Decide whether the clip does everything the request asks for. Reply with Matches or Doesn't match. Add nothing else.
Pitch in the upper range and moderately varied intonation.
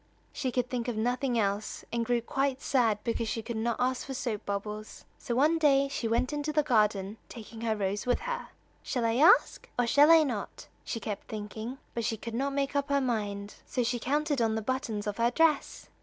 Matches